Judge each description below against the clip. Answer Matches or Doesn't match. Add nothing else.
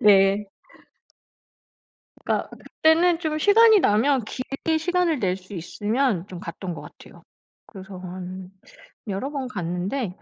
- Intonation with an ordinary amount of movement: Doesn't match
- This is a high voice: Matches